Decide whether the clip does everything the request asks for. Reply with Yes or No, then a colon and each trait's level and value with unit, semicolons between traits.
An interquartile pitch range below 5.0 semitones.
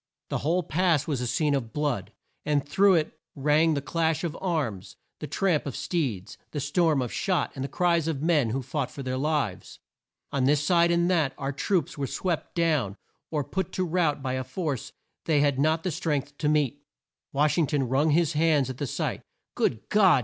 Yes: average, 3.5 semitones